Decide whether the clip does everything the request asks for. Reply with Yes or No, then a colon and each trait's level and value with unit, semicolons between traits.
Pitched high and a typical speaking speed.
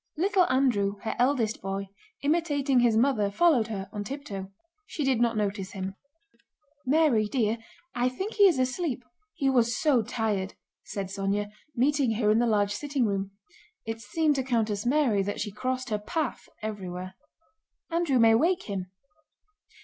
Yes: high, 235 Hz; average, 155 wpm